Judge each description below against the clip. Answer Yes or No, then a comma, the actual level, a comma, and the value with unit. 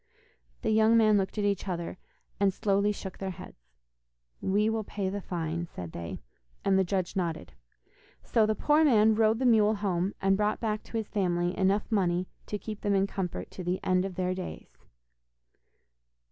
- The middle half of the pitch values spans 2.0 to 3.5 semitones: Yes, average, 2.8 semitones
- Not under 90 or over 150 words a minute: No, average, 185 wpm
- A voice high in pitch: Yes, high, 195 Hz